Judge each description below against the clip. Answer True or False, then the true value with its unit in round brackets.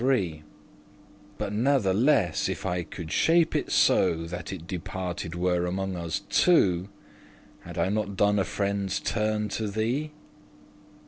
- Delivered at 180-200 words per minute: False (140 wpm)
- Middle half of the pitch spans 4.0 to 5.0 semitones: False (3.5 semitones)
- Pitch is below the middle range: True (95 Hz)